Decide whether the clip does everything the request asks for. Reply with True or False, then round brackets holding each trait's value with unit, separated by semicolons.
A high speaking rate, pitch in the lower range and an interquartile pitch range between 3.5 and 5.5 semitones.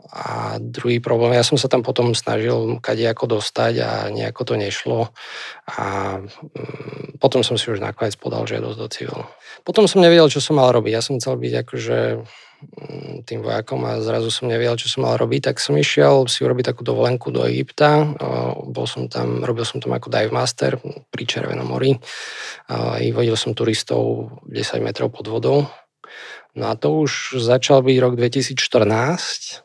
True (175 wpm; 120 Hz; 5.2 semitones)